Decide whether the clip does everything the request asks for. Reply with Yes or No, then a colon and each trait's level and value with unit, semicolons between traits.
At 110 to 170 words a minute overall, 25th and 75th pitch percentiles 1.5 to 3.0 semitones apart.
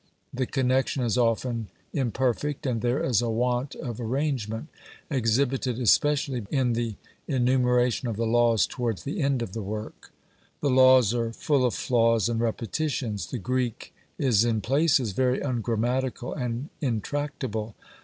Yes: average, 145 wpm; narrow, 2.4 semitones